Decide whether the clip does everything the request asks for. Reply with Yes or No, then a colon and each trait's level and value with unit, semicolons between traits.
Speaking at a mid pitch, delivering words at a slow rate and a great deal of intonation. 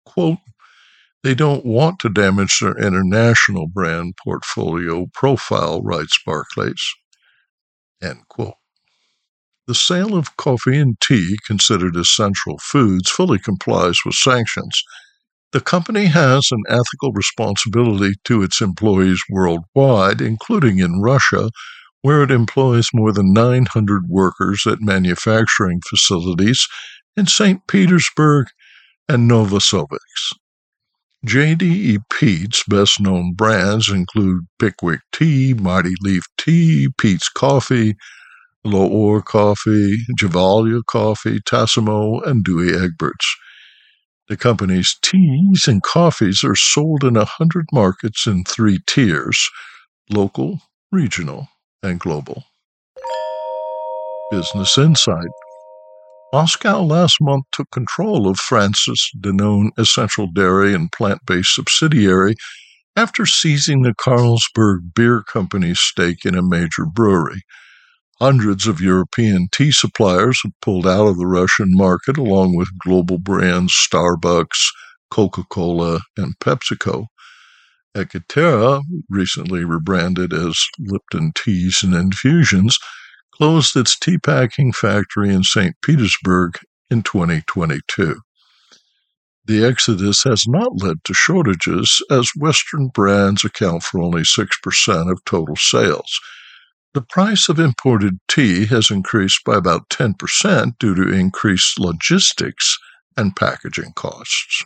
No: low, 110 Hz; slow, 110 wpm; wide, 6.3 semitones